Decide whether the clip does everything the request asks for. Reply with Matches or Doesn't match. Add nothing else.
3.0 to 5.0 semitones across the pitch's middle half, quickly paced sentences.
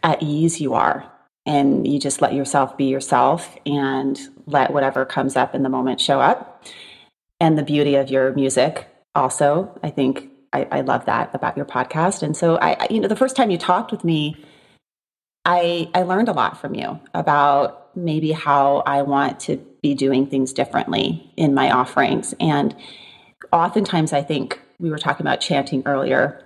Doesn't match